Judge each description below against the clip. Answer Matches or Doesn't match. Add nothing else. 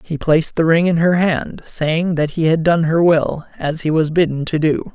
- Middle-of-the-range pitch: Matches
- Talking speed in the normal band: Doesn't match